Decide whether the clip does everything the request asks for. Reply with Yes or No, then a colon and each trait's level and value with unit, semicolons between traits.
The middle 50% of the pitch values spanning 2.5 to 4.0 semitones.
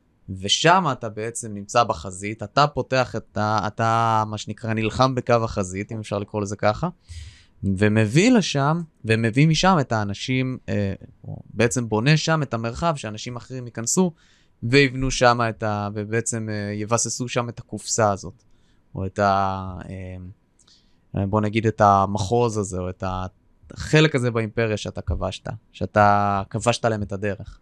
Yes: average, 3.4 semitones